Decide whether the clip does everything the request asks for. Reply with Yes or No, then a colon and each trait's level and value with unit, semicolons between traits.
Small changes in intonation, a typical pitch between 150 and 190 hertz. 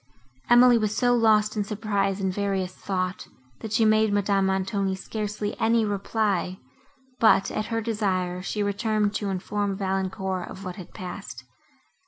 No: narrow, 2.2 semitones; high, 205 Hz